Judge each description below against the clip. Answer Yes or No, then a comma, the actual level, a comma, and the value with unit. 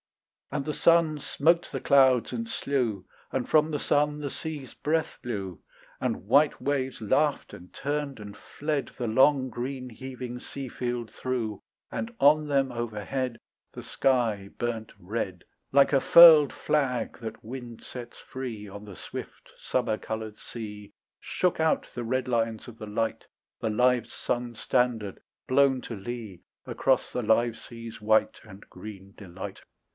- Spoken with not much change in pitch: No, average, 4.0 semitones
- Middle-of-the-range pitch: No, low, 125 Hz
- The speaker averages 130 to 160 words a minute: Yes, average, 150 wpm